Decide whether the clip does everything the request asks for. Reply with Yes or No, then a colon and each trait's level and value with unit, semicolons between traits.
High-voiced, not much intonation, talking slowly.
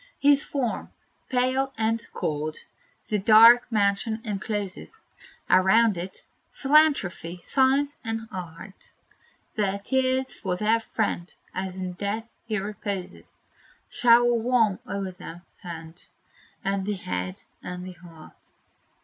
No: high, 210 Hz; average, 4.5 semitones; slow, 115 wpm